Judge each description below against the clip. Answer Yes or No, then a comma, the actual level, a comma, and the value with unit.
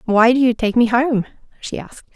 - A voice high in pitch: Yes, high, 235 Hz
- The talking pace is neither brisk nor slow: No, fast, 225 wpm